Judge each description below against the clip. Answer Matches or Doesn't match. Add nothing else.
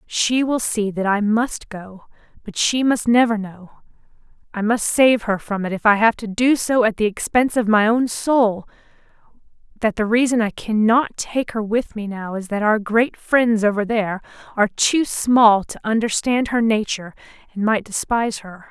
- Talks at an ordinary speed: Matches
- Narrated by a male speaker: Doesn't match